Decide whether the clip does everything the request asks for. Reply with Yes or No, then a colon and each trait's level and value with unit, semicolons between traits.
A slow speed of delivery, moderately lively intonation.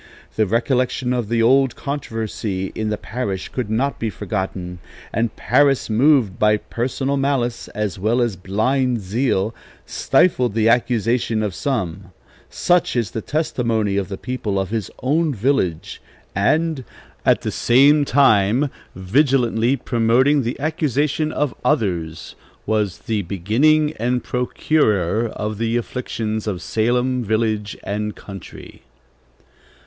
Yes: slow, 130 wpm; average, 4.2 semitones